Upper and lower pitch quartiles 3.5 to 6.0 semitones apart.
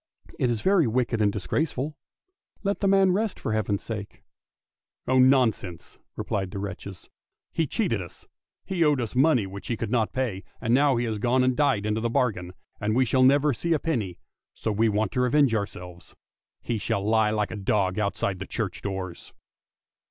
Yes: average, 4.5 semitones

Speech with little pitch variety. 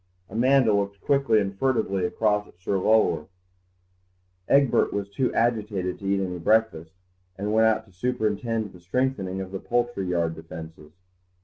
No: average, 3.5 semitones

